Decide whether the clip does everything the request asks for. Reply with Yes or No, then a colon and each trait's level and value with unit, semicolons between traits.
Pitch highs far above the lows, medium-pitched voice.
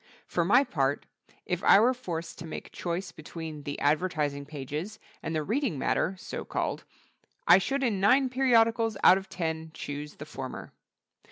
Yes: wide, 6.5 semitones; medium, 175 Hz